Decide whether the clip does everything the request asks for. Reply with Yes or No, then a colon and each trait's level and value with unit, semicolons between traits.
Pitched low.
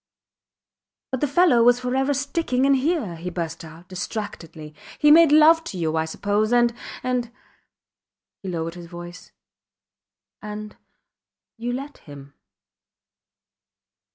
No: high, 225 Hz